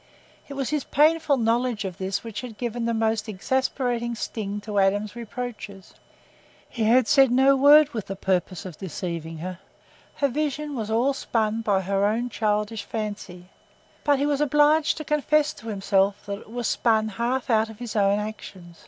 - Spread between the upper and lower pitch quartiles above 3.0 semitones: Yes, average, 4.5 semitones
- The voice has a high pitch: Yes, high, 225 Hz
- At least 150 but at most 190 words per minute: Yes, average, 170 wpm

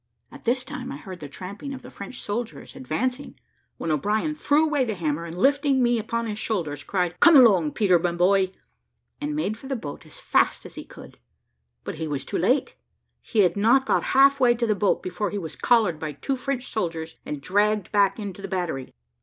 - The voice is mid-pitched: No, high, 210 Hz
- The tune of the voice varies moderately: No, wide, 6.2 semitones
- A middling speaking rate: No, fast, 210 wpm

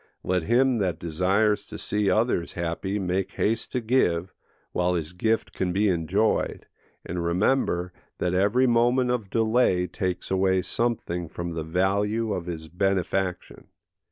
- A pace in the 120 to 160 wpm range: Yes, average, 145 wpm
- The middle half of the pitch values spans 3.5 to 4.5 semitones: Yes, average, 3.8 semitones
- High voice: No, very low, 95 Hz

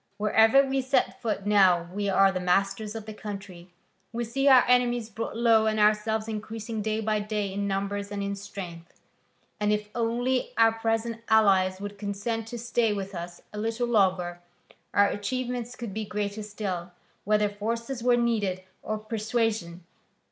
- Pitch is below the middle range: No, high, 215 Hz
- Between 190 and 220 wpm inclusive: No, average, 165 wpm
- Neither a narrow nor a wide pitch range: No, narrow, 2.3 semitones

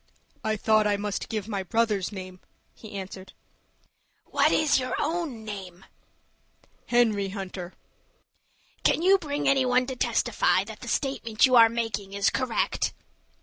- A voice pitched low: No, high, 220 Hz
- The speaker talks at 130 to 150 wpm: Yes, average, 145 wpm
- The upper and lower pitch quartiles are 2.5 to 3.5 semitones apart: No, average, 4.4 semitones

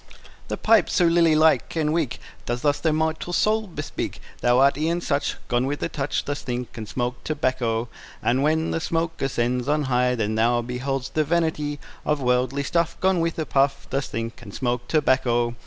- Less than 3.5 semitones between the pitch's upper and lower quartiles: No, average, 4.4 semitones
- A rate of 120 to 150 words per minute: No, average, 190 wpm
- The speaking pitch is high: No, medium, 140 Hz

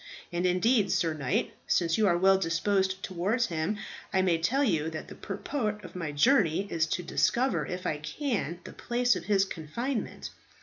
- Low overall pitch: No, medium, 185 Hz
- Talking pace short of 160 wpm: No, average, 180 wpm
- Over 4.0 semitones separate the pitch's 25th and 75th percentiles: Yes, average, 4.6 semitones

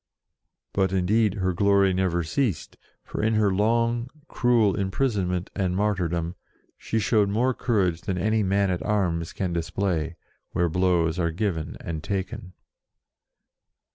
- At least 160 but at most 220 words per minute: No, average, 140 wpm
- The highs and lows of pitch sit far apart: No, average, 3.3 semitones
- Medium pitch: No, very low, 95 Hz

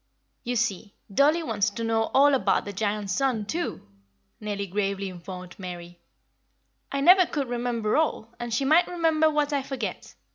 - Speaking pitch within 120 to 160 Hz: No, high, 235 Hz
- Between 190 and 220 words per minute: No, average, 155 wpm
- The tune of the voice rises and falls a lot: Yes, wide, 6.0 semitones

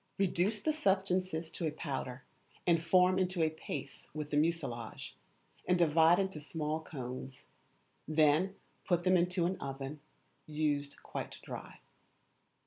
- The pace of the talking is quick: No, slow, 135 wpm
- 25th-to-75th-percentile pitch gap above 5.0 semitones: No, average, 3.7 semitones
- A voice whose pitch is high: No, medium, 160 Hz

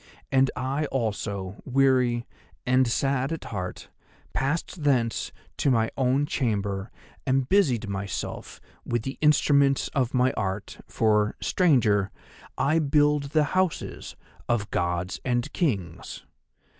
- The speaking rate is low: Yes, slow, 120 wpm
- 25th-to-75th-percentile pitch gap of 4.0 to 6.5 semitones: Yes, average, 5.0 semitones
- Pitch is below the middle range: Yes, low, 130 Hz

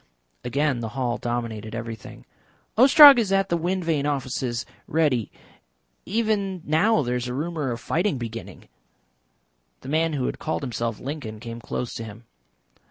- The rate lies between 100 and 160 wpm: Yes, average, 155 wpm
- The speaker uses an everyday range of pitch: No, wide, 6.2 semitones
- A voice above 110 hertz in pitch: Yes, low, 135 Hz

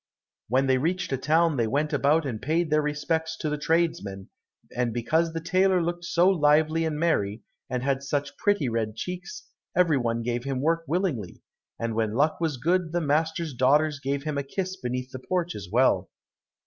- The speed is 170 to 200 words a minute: Yes, average, 190 wpm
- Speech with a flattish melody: No, average, 4.5 semitones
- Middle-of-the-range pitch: Yes, medium, 150 Hz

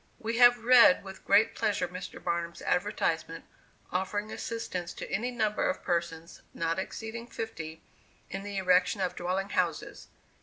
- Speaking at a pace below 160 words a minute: Yes, average, 145 wpm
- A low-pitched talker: No, high, 190 Hz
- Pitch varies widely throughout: No, average, 4.3 semitones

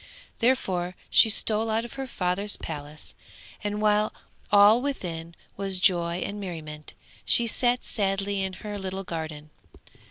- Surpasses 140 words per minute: No, slow, 135 wpm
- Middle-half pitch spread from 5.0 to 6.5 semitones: No, average, 3.6 semitones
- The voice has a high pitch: Yes, high, 195 Hz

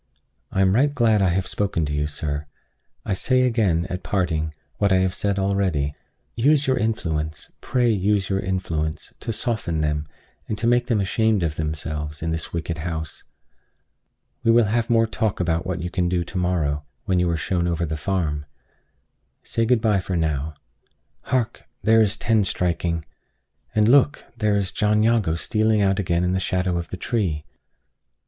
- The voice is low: Yes, very low, 95 Hz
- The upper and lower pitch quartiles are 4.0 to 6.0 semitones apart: Yes, average, 5.0 semitones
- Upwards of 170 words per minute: Yes, average, 180 wpm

